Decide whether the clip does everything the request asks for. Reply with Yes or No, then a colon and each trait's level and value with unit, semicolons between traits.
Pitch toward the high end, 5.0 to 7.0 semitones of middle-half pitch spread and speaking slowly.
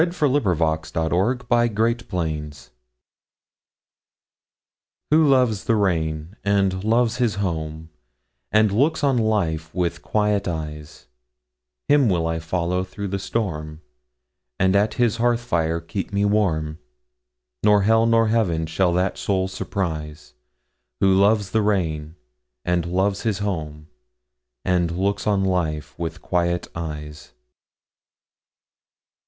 No: very low, 90 Hz; average, 5.3 semitones; slow, 105 wpm